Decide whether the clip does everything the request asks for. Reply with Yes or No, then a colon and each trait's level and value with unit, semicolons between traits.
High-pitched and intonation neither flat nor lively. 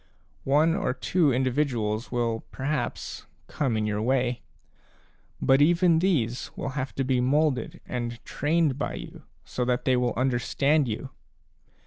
No: low, 130 Hz; average, 3.6 semitones